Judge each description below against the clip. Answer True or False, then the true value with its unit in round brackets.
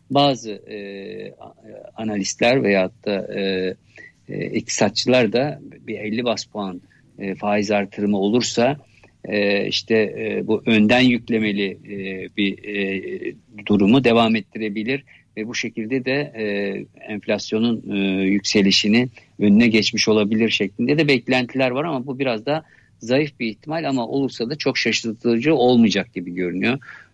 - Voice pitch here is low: True (110 Hz)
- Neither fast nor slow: True (130 wpm)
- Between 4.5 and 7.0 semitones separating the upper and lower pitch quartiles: False (3.3 semitones)